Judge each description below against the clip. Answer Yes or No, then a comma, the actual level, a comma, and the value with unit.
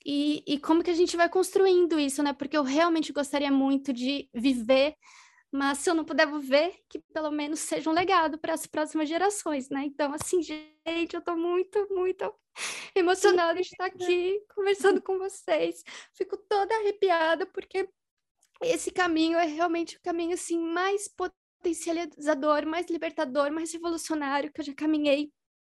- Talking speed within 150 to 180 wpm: Yes, average, 165 wpm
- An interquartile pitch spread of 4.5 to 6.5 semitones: No, average, 3.6 semitones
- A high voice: Yes, very high, 335 Hz